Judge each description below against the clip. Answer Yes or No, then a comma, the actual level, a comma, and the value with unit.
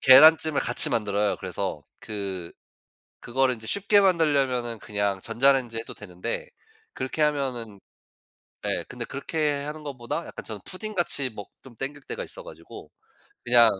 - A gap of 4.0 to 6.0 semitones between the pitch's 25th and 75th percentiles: Yes, average, 5.2 semitones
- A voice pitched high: No, low, 130 Hz